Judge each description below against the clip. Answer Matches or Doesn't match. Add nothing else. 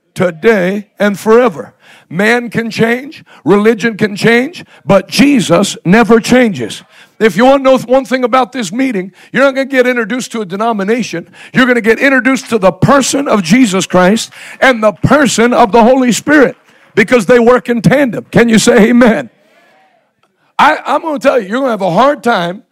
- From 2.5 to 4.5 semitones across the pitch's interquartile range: Matches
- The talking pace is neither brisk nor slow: Matches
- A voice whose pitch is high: Matches